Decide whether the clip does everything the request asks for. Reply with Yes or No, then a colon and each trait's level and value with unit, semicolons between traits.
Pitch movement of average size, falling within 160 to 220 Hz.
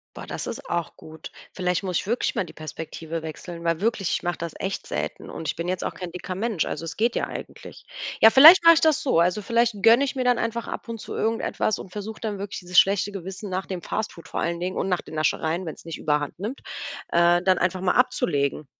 Yes: average, 4.7 semitones; medium, 185 Hz